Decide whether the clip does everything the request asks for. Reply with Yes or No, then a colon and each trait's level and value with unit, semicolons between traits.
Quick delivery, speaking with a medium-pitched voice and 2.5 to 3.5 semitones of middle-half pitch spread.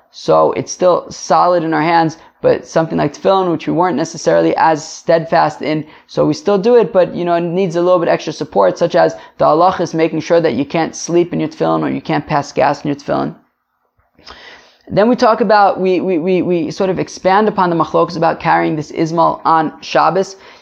Yes: fast, 220 wpm; medium, 170 Hz; average, 2.8 semitones